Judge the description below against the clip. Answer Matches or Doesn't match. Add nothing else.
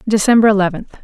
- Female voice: Matches